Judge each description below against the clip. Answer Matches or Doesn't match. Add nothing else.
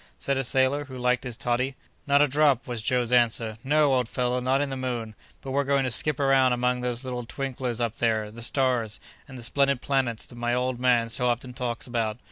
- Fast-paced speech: Matches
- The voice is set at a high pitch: Doesn't match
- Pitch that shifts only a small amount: Matches